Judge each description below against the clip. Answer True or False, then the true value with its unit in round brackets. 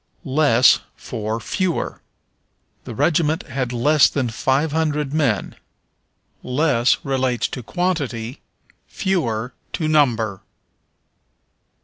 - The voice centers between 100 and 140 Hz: True (135 Hz)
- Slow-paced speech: True (90 wpm)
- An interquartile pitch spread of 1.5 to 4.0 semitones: False (4.7 semitones)